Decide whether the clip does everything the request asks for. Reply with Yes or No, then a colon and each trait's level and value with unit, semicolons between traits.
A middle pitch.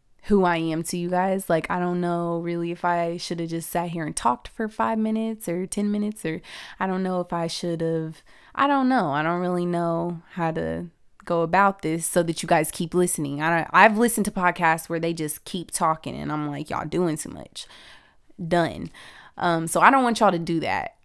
Yes: medium, 170 Hz